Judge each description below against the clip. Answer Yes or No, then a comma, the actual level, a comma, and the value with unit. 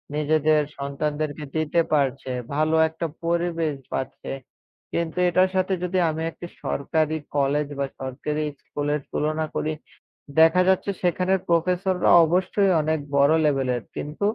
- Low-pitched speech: No, medium, 155 Hz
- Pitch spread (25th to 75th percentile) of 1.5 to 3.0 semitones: Yes, average, 2.7 semitones